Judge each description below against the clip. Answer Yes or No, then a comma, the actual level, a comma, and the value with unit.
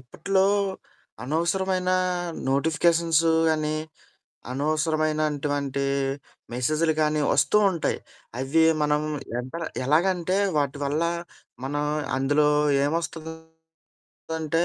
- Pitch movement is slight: Yes, narrow, 2.2 semitones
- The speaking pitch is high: No, medium, 155 Hz